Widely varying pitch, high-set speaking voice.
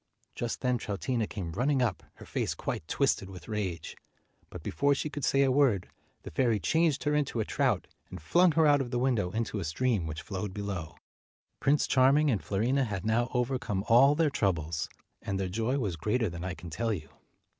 No: wide, 6.0 semitones; low, 115 Hz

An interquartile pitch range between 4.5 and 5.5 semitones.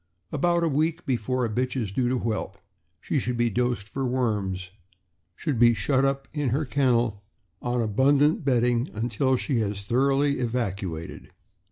No: average, 3.6 semitones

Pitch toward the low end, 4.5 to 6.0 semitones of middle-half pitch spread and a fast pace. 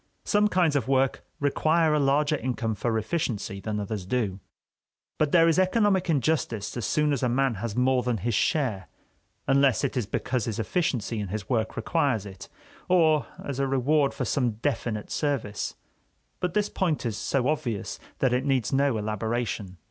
No: low, 130 Hz; average, 5.3 semitones; average, 175 wpm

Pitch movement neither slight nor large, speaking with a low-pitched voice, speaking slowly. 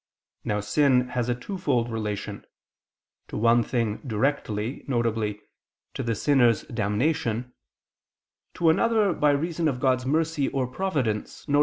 Yes: average, 4.5 semitones; low, 125 Hz; slow, 130 wpm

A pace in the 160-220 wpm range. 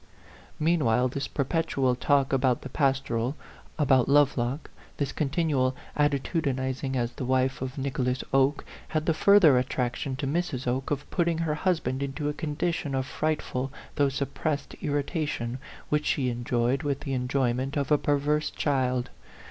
No: average, 150 wpm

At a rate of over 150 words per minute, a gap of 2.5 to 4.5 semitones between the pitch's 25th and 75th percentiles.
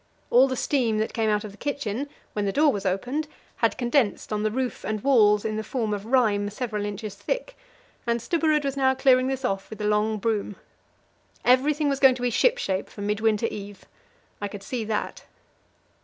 Yes: average, 200 wpm; average, 4.1 semitones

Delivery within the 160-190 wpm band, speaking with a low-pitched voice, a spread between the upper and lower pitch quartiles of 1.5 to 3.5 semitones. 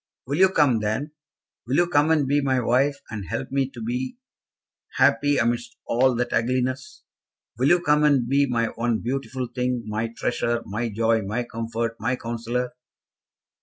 Yes: average, 165 wpm; low, 125 Hz; average, 2.9 semitones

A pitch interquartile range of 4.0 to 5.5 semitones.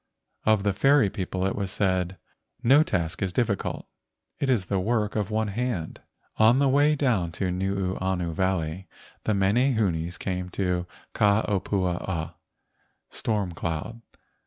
No: average, 3.4 semitones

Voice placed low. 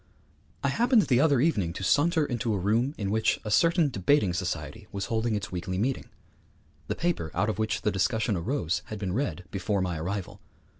Yes: low, 105 Hz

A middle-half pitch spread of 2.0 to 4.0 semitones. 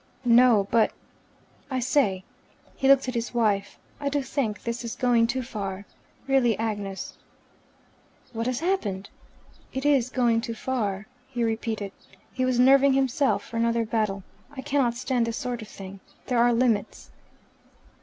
Yes: average, 3.1 semitones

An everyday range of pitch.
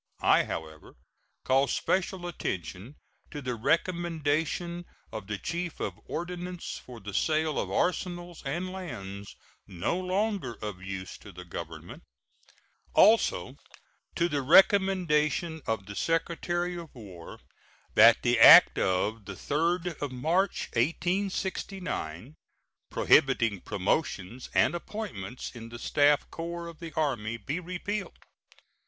No: wide, 8.3 semitones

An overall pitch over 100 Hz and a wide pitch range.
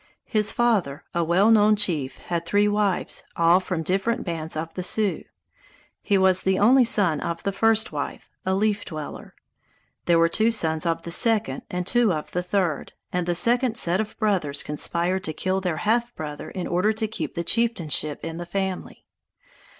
No: medium, 185 Hz; average, 4.2 semitones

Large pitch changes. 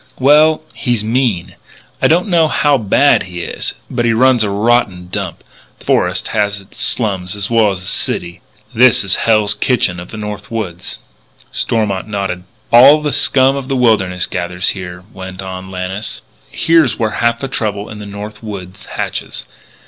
No: average, 4.5 semitones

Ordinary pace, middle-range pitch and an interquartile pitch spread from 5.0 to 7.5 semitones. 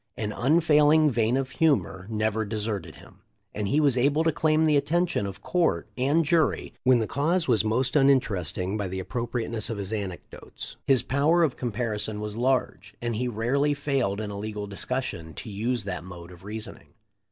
No: average, 180 wpm; low, 120 Hz; average, 5.3 semitones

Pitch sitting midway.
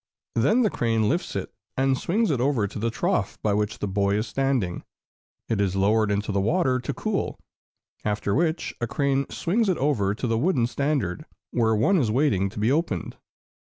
No: low, 115 Hz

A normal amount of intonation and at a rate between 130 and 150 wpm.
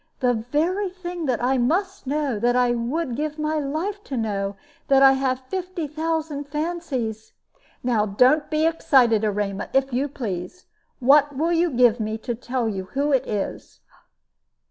No: average, 4.8 semitones; average, 165 wpm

